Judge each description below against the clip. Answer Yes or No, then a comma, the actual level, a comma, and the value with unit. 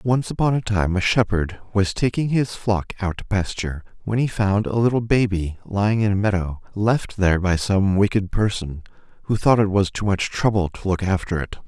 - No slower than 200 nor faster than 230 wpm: Yes, fast, 205 wpm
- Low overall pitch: Yes, low, 100 Hz